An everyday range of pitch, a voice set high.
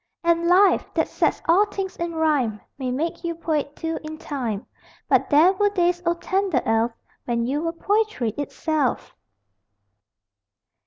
Yes: average, 4.7 semitones; very high, 325 Hz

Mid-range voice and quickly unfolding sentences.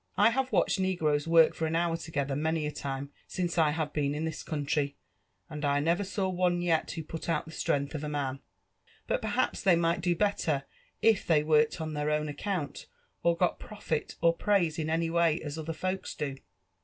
Yes: medium, 160 Hz; fast, 210 wpm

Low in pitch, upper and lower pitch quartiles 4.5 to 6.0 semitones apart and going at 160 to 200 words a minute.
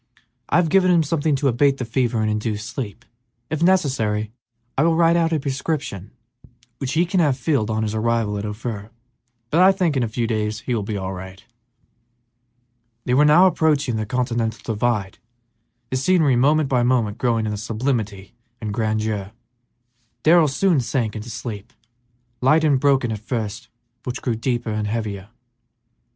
Yes: low, 120 Hz; average, 5.2 semitones; average, 175 wpm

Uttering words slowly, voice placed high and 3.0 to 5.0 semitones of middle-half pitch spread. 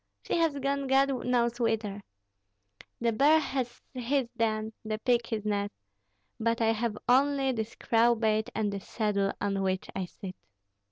No: average, 155 wpm; high, 230 Hz; average, 3.3 semitones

